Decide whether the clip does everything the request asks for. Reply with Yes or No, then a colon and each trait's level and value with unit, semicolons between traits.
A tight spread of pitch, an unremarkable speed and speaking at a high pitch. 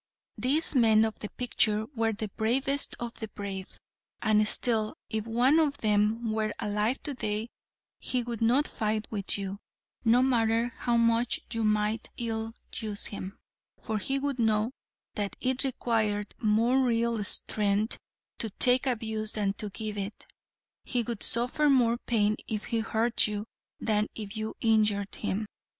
Yes: narrow, 2.1 semitones; average, 155 wpm; high, 220 Hz